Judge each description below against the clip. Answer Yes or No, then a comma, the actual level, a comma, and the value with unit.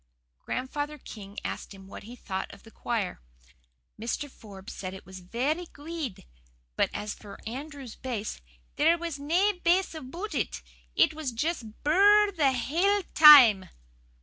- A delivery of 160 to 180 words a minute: Yes, average, 165 wpm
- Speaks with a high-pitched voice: Yes, very high, 275 Hz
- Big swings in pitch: Yes, wide, 7.3 semitones